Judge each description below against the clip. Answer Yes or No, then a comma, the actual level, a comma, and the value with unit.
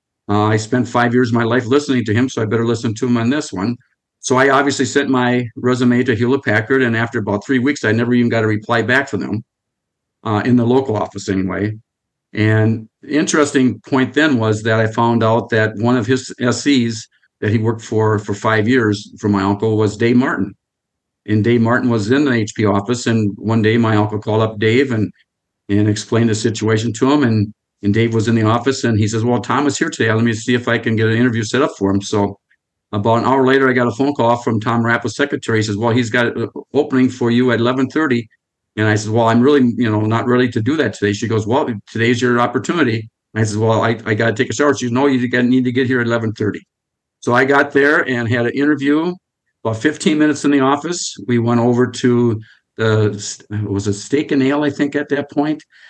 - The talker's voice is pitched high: No, low, 120 Hz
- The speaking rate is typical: No, fast, 240 wpm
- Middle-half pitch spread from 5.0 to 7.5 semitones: No, average, 2.9 semitones